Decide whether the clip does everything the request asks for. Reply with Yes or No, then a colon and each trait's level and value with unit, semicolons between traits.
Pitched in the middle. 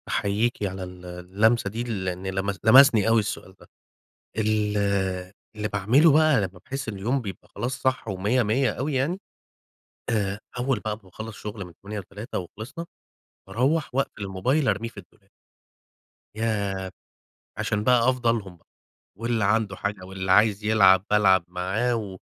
No: low, 105 Hz